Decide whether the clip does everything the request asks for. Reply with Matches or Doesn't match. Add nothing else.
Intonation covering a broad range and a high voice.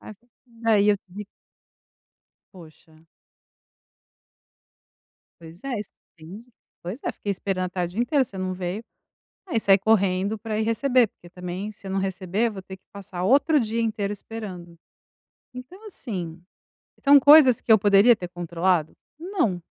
Doesn't match